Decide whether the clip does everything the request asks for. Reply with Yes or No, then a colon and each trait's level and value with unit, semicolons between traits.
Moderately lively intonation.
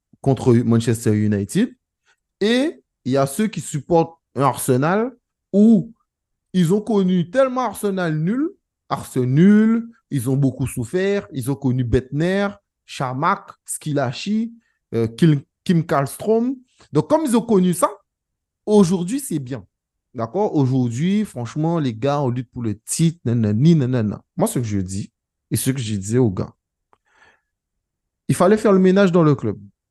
No: wide, 8.2 semitones